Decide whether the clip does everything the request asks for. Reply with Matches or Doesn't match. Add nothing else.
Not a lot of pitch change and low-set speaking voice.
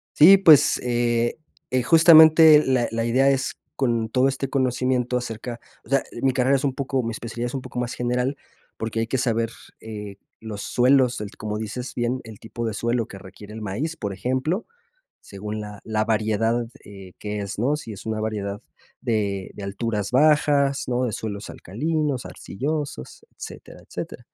Doesn't match